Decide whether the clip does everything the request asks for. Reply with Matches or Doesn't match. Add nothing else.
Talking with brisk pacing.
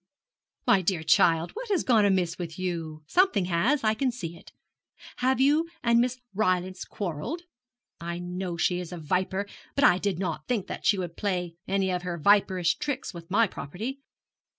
Doesn't match